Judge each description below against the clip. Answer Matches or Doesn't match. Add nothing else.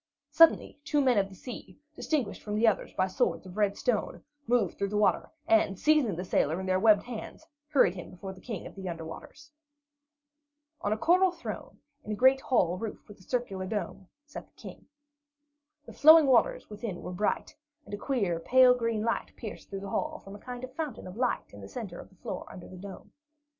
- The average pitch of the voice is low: Doesn't match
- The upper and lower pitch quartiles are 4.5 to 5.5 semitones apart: Matches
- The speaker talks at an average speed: Doesn't match